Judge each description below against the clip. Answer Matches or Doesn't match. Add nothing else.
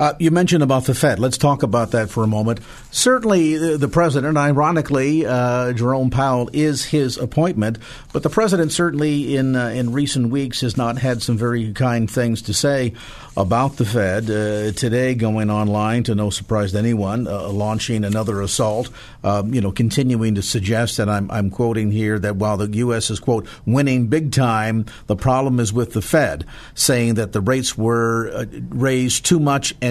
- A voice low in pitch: Matches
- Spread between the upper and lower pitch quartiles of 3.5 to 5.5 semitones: Matches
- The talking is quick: Doesn't match